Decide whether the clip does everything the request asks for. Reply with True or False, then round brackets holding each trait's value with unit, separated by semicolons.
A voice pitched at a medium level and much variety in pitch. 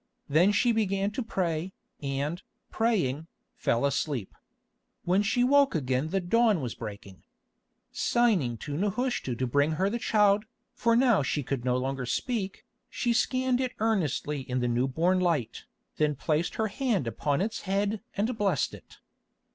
True (180 Hz; 8.1 semitones)